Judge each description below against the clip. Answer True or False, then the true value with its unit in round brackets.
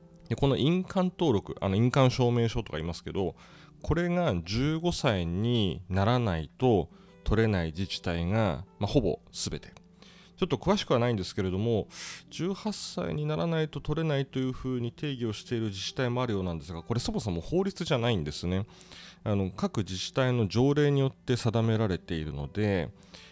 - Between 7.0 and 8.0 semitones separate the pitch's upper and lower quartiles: True (7.4 semitones)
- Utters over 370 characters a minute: False (360 characters per minute)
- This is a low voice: True (115 Hz)